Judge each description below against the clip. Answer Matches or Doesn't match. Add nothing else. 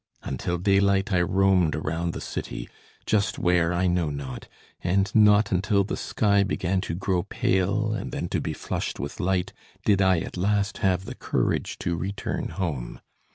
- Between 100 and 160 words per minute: Doesn't match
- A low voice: Matches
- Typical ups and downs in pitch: Doesn't match